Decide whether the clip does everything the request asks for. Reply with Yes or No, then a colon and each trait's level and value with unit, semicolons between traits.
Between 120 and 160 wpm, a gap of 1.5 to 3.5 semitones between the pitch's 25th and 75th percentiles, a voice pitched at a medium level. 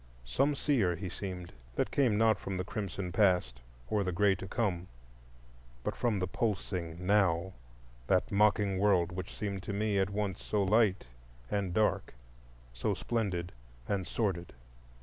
No: average, 150 wpm; average, 2.8 semitones; very low, 95 Hz